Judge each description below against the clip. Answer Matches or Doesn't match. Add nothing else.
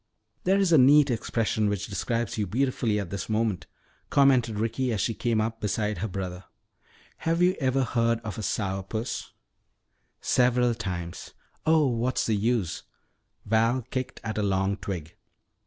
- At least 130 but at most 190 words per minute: Matches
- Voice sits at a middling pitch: Doesn't match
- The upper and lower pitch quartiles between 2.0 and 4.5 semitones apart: Matches